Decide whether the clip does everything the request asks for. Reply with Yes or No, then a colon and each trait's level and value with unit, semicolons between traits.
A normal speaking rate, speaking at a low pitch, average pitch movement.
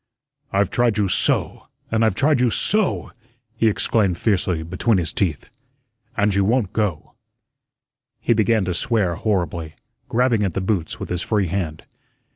Yes: average, 155 wpm; low, 100 Hz; average, 3.9 semitones